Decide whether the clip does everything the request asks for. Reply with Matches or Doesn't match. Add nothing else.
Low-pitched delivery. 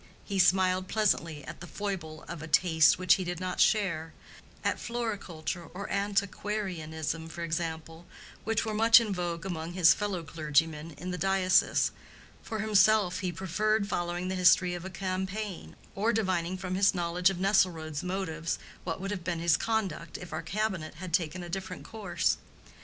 Doesn't match